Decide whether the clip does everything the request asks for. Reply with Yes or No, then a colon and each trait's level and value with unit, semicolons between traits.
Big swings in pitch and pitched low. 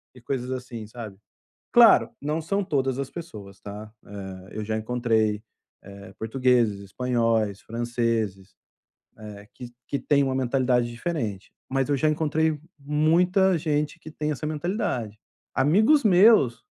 Yes: wide, 5.8 semitones; low, 125 Hz